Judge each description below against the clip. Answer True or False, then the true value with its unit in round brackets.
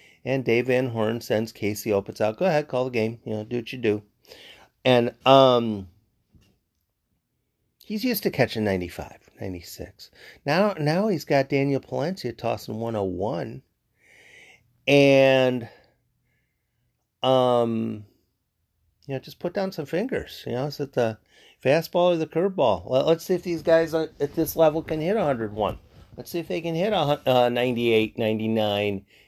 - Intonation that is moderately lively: False (5.9 semitones)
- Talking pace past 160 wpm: False (150 wpm)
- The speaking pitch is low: True (125 Hz)